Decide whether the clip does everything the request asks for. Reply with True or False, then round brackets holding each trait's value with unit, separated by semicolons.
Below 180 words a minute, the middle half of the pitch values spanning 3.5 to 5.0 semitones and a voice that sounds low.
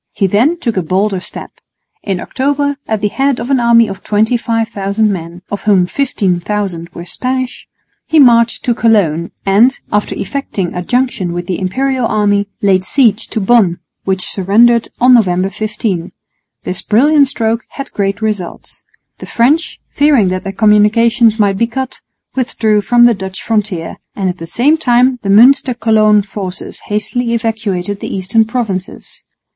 False (160 wpm; 3.8 semitones; 215 Hz)